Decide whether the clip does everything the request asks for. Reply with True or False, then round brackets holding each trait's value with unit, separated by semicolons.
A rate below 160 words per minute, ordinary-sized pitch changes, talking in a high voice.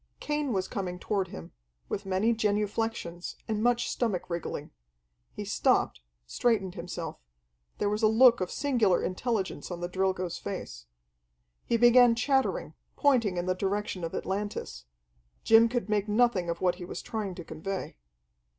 True (150 wpm; 4.2 semitones; 200 Hz)